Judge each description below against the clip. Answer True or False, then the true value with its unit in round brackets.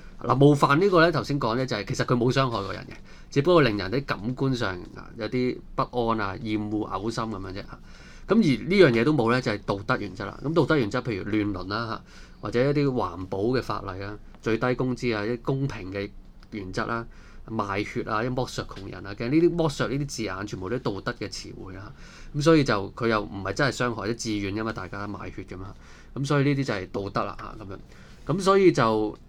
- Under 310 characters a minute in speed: False (350 characters per minute)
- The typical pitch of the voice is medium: False (115 Hz)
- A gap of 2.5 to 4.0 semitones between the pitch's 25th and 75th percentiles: False (4.4 semitones)